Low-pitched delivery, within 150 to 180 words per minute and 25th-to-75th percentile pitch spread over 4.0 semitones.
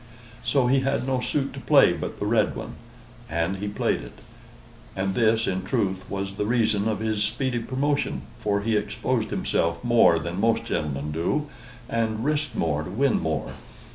Yes: low, 110 Hz; average, 175 wpm; average, 4.8 semitones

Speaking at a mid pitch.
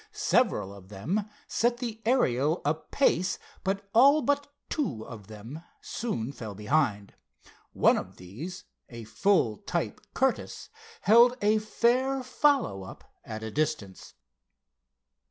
Yes: medium, 160 Hz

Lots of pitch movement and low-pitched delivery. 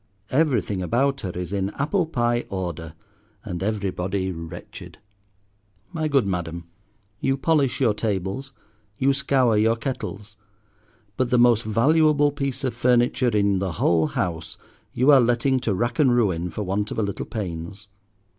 Yes: wide, 5.8 semitones; low, 110 Hz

